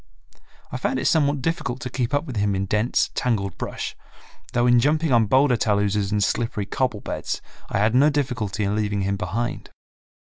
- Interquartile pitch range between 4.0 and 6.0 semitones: Yes, average, 4.3 semitones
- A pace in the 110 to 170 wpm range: No, average, 185 wpm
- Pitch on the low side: Yes, low, 115 Hz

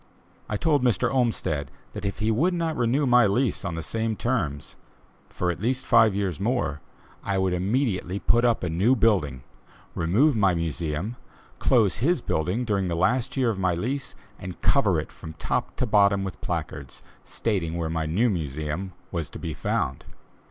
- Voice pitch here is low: Yes, low, 100 Hz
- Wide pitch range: Yes, wide, 6.2 semitones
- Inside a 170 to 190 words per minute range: Yes, average, 180 wpm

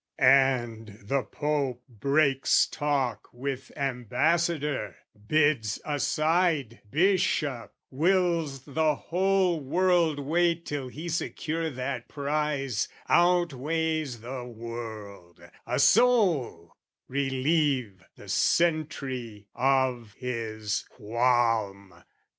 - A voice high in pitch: No, low, 135 Hz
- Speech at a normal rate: No, slow, 85 wpm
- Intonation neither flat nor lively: Yes, average, 4.9 semitones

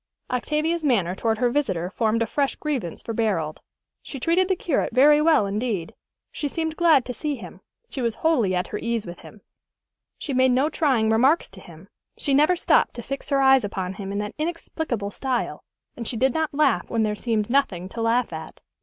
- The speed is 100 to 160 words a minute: No, fast, 205 wpm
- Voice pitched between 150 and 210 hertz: No, high, 245 Hz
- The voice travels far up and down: Yes, wide, 5.8 semitones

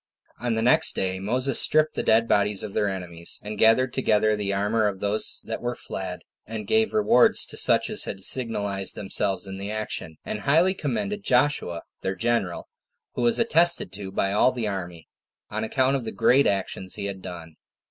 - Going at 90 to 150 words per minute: No, average, 195 wpm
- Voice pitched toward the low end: Yes, low, 105 Hz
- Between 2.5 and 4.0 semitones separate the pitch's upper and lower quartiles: No, average, 4.4 semitones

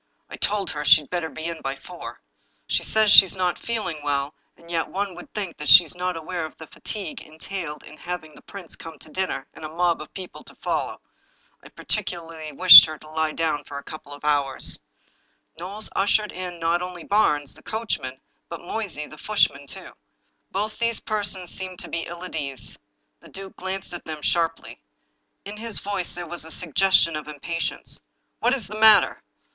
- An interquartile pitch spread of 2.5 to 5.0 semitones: Yes, average, 3.9 semitones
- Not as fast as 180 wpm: No, average, 200 wpm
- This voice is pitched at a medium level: Yes, medium, 170 Hz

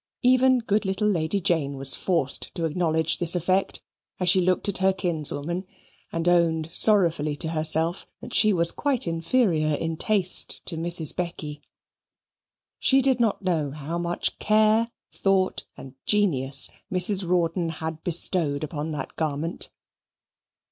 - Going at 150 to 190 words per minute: No, average, 140 wpm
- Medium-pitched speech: Yes, medium, 170 Hz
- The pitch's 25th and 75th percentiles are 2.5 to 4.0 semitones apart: Yes, average, 3.4 semitones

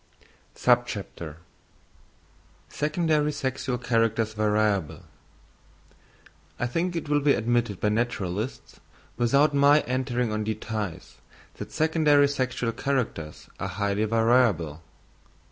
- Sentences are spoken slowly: Yes, slow, 90 wpm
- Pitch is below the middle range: Yes, low, 120 Hz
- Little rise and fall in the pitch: No, average, 4.9 semitones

